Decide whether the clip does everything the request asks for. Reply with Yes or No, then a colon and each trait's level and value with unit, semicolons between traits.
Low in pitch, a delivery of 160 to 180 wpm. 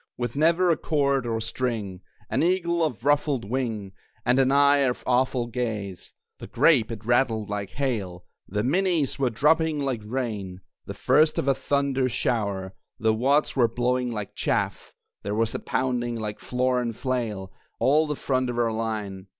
Yes: low, 125 Hz; average, 165 wpm